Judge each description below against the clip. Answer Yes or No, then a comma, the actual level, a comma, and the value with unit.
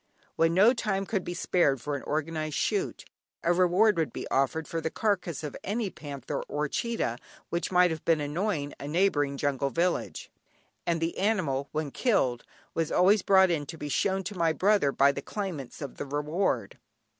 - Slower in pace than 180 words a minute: No, average, 185 wpm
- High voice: No, medium, 165 Hz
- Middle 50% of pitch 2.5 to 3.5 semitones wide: No, average, 4.8 semitones